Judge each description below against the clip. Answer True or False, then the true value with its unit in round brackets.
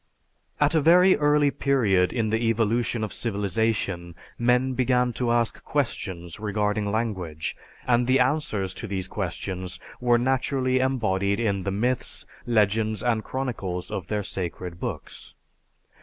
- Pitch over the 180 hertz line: False (110 Hz)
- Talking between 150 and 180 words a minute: False (135 wpm)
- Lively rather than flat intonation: False (4.3 semitones)